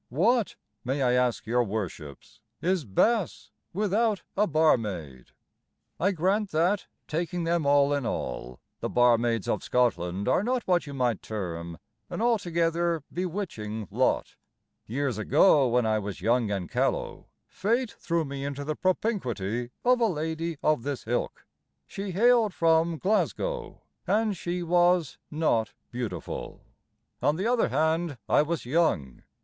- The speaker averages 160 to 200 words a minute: No, average, 140 wpm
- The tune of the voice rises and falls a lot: Yes, wide, 7.5 semitones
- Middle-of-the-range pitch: Yes, medium, 155 Hz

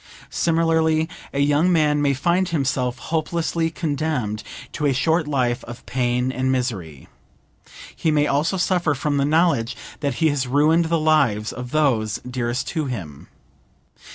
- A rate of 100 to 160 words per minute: Yes, average, 150 wpm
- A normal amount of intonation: Yes, average, 4.3 semitones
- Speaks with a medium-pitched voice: Yes, medium, 145 Hz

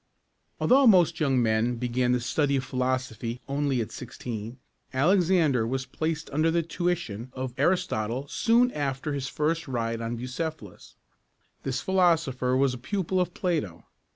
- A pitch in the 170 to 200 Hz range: No, low, 135 Hz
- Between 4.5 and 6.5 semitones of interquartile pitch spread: Yes, average, 5.1 semitones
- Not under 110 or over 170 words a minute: Yes, average, 150 wpm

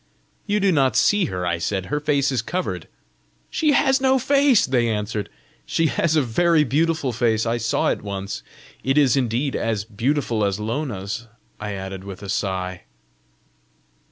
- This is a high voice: No, low, 120 Hz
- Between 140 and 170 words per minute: Yes, average, 165 wpm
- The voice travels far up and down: Yes, wide, 7.1 semitones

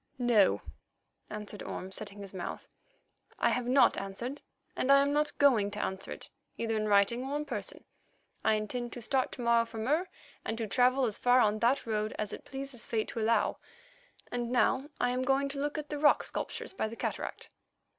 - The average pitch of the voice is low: No, high, 240 Hz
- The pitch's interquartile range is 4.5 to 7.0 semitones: No, average, 4.0 semitones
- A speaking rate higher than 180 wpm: Yes, average, 200 wpm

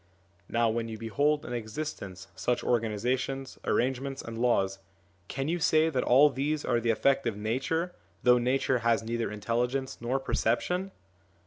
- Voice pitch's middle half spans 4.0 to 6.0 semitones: No, average, 3.0 semitones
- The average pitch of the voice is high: No, low, 125 Hz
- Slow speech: No, average, 155 wpm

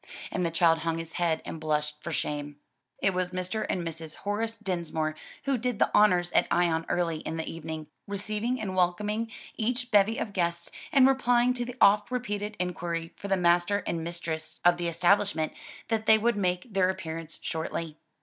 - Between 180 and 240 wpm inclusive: Yes, average, 185 wpm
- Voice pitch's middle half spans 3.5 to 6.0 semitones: Yes, average, 4.3 semitones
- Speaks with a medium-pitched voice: Yes, medium, 180 Hz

